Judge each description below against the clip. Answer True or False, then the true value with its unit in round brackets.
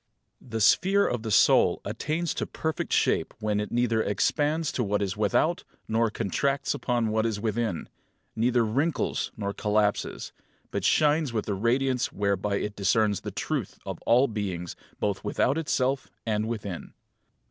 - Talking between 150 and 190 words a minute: True (160 wpm)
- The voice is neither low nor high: False (110 Hz)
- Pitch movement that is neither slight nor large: True (4.1 semitones)